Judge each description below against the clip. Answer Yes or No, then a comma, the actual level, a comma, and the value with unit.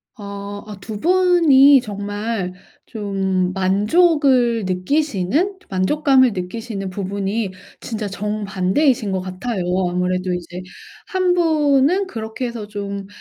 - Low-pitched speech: No, high, 210 Hz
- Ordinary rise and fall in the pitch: No, wide, 5.9 semitones